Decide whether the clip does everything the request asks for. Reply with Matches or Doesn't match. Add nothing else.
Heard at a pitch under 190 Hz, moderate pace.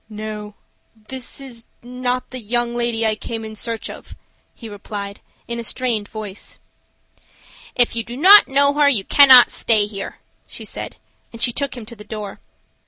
Doesn't match